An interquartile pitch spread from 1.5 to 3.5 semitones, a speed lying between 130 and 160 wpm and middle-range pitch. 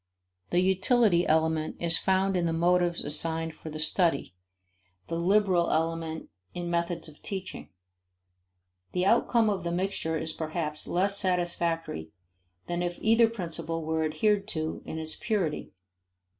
Yes: average, 2.8 semitones; average, 140 wpm; medium, 170 Hz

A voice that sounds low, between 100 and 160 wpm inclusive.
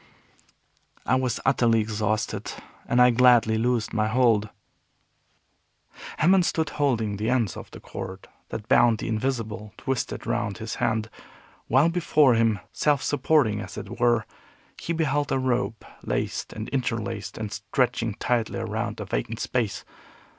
Yes: low, 115 Hz; average, 140 wpm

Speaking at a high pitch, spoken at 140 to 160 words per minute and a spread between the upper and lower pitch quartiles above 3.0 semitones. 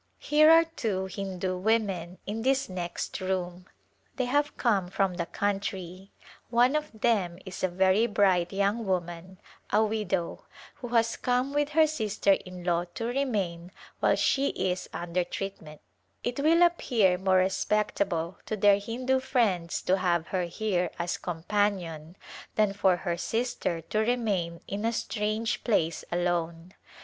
Yes: high, 195 Hz; average, 155 wpm; average, 4.4 semitones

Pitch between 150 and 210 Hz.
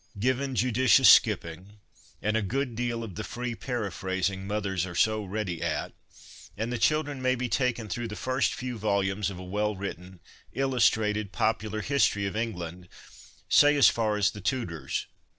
No: low, 110 Hz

